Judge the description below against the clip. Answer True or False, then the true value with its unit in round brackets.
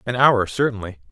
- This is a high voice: False (115 Hz)